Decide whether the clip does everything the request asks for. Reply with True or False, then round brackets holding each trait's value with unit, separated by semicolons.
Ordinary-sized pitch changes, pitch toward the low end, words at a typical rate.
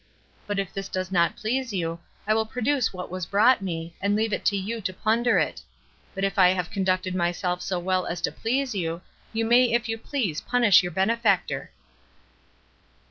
False (3.7 semitones; 195 Hz; 190 wpm)